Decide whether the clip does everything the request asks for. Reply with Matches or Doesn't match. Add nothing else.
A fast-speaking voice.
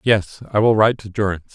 Matches